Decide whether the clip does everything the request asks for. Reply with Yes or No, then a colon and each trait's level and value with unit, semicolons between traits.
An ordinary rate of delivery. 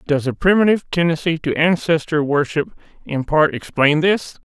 Yes: average, 150 wpm